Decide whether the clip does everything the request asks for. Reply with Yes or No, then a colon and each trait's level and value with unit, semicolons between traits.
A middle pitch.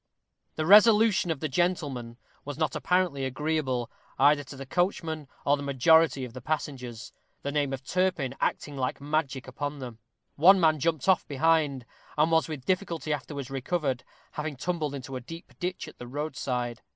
Yes: medium, 145 Hz